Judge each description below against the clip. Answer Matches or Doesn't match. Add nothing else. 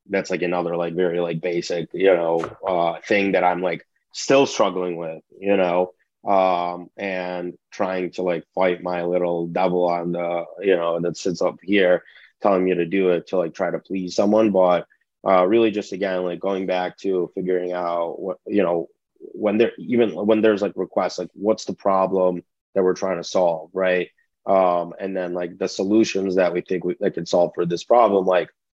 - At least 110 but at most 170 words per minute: Doesn't match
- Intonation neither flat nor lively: Doesn't match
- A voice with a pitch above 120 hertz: Doesn't match